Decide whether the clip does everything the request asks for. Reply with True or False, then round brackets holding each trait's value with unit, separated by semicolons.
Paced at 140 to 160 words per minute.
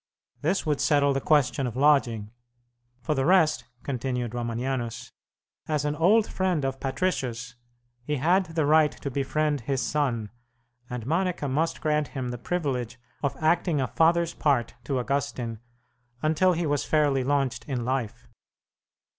True (145 wpm)